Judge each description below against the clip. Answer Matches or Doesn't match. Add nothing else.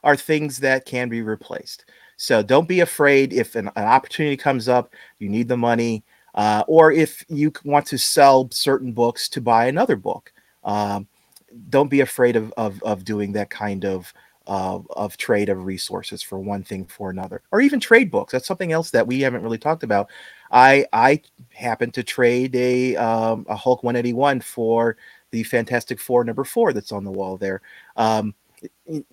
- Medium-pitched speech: Doesn't match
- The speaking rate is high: Doesn't match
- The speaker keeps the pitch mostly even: Doesn't match